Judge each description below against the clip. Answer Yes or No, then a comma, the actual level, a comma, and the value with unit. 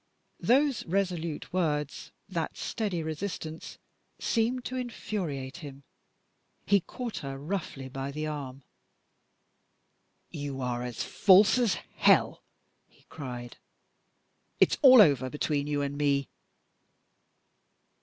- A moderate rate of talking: No, slow, 105 wpm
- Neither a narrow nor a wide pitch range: No, wide, 6.3 semitones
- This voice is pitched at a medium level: Yes, medium, 155 Hz